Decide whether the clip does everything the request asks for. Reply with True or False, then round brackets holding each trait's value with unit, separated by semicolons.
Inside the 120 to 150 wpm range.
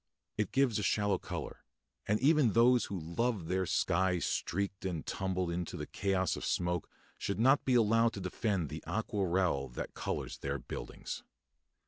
False (160 wpm)